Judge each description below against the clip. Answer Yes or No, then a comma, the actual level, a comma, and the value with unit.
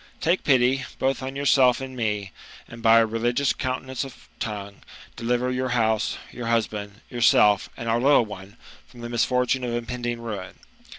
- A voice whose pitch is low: Yes, low, 120 Hz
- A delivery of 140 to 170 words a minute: Yes, average, 165 wpm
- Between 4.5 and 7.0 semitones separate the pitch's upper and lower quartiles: No, narrow, 2.5 semitones